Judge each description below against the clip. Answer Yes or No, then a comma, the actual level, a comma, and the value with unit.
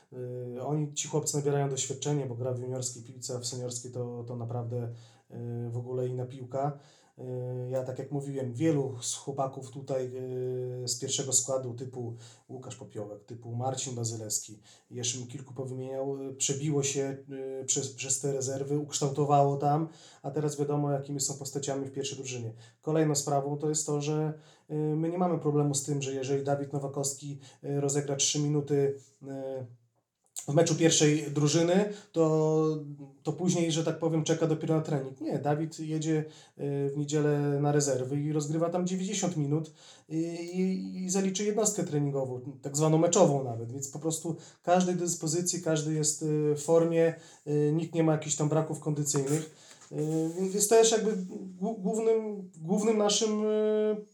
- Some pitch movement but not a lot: Yes, average, 3.1 semitones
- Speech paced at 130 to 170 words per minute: Yes, average, 150 wpm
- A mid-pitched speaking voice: Yes, medium, 145 Hz